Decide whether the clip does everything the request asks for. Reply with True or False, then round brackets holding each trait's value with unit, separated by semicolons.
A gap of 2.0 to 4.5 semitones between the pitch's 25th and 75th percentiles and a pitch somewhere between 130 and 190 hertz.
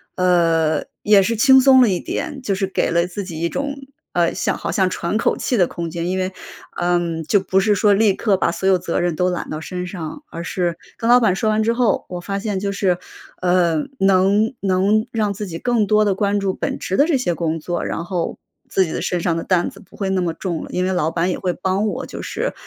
True (3.1 semitones; 185 Hz)